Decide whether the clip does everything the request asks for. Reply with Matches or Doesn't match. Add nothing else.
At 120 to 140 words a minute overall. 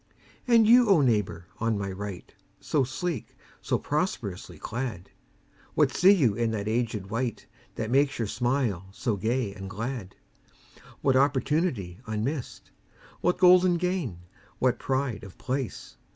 Matches